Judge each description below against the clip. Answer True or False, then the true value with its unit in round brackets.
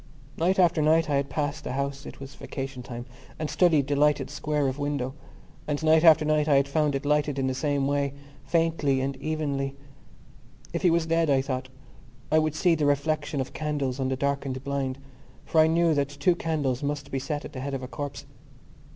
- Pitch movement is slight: True (2.2 semitones)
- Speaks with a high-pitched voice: False (145 Hz)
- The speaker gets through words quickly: True (210 wpm)